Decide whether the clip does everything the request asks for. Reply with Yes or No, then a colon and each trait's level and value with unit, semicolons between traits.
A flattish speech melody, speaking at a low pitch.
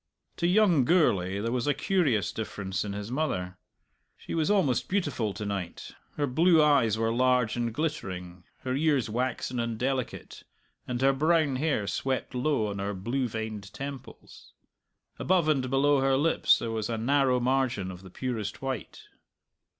No: average, 5.0 semitones; low, 125 Hz